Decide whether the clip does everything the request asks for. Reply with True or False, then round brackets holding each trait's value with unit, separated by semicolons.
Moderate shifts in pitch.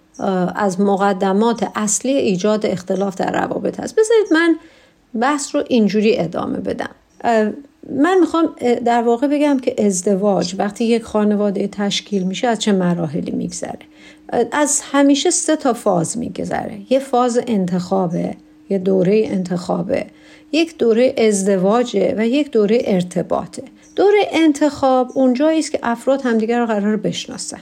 False (5.8 semitones)